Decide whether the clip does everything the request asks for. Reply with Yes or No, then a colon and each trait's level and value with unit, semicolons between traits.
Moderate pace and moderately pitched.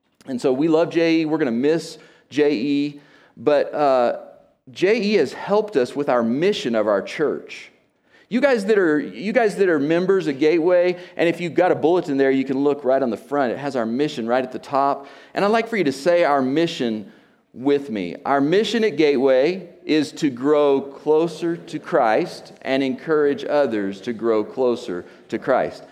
Yes: average, 195 wpm; medium, 150 Hz